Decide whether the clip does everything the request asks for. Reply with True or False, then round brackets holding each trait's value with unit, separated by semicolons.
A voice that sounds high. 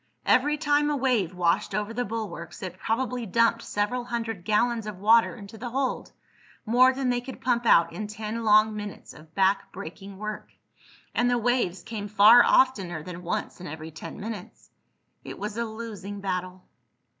True (215 Hz)